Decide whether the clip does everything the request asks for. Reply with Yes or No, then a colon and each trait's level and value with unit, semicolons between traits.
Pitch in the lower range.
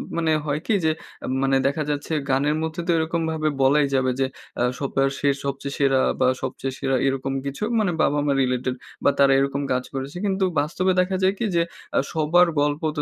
No: medium, 145 Hz